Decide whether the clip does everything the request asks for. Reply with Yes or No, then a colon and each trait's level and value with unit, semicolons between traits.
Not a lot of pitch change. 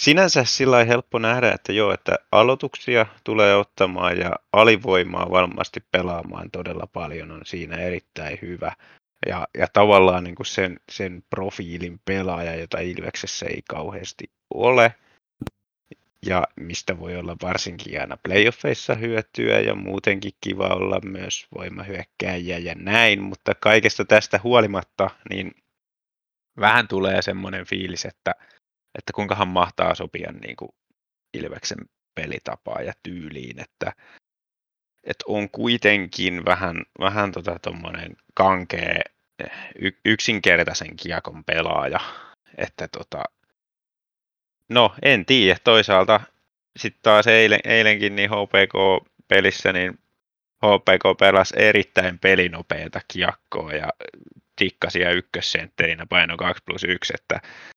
No: average, 3.1 semitones